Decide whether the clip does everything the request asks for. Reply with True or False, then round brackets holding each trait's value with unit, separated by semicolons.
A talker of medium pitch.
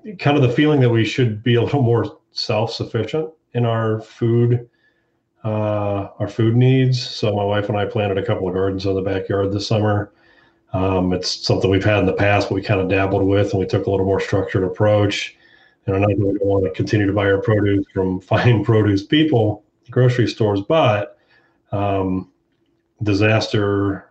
False (105 Hz)